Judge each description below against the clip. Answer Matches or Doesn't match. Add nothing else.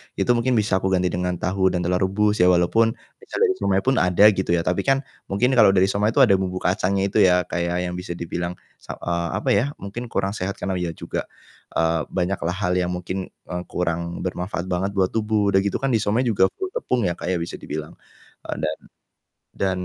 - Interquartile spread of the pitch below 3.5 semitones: Matches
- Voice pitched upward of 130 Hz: Doesn't match